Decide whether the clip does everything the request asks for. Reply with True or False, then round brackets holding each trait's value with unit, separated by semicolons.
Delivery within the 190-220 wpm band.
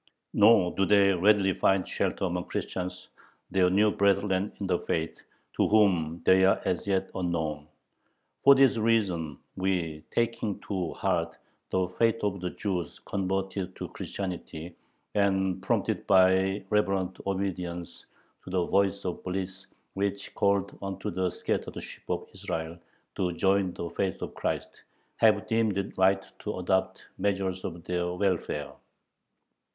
False (140 wpm)